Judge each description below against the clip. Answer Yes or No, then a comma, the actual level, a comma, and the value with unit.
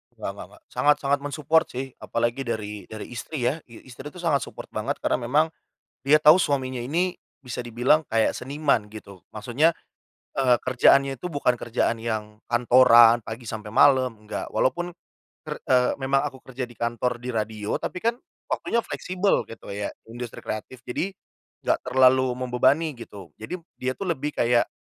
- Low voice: Yes, low, 125 Hz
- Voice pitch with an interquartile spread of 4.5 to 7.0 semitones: No, average, 3.5 semitones